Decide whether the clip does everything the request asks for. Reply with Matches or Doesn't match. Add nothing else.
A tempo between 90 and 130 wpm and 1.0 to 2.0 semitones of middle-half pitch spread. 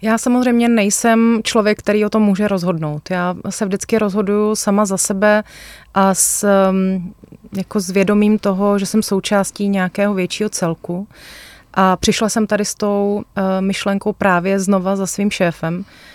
Doesn't match